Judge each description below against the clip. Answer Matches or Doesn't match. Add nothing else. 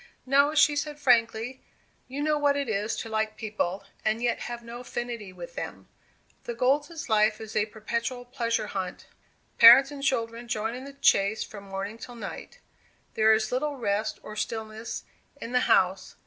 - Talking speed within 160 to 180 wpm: Matches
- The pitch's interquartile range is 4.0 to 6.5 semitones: Doesn't match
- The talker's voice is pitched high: Matches